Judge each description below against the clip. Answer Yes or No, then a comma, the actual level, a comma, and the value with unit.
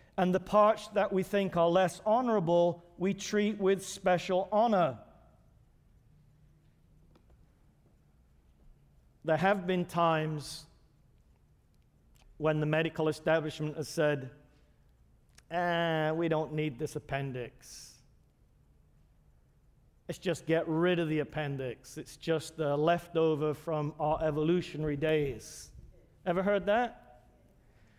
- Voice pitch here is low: No, medium, 155 Hz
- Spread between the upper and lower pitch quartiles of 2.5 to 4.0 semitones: Yes, average, 3.2 semitones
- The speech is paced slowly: Yes, slow, 105 wpm